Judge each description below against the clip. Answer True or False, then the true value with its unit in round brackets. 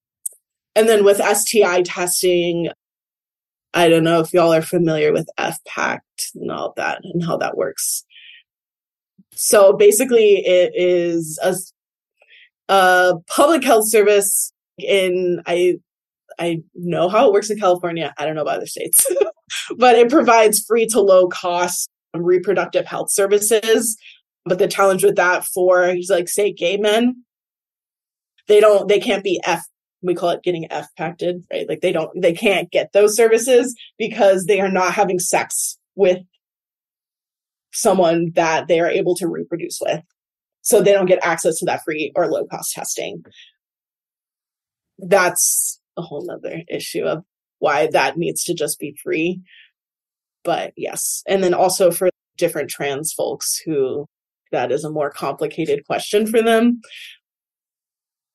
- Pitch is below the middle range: False (190 Hz)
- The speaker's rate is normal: True (145 wpm)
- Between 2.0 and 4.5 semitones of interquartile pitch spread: True (3.8 semitones)